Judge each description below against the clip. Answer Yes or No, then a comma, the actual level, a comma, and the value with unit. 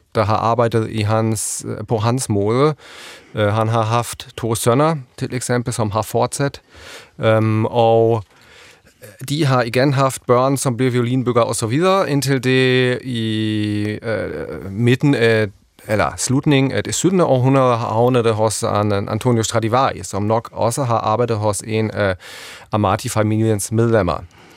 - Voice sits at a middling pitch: No, low, 115 Hz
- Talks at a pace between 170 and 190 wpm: No, slow, 145 wpm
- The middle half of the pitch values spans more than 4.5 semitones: No, average, 3.0 semitones